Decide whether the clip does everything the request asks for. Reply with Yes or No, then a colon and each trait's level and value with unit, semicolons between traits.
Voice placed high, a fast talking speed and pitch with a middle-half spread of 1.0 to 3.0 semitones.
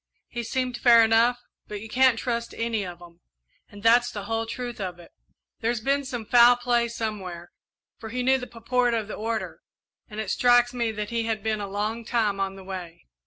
Yes: high, 225 Hz; fast, 210 wpm; average, 2.7 semitones